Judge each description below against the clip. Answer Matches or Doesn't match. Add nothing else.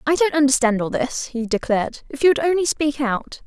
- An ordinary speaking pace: Doesn't match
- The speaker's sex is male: Doesn't match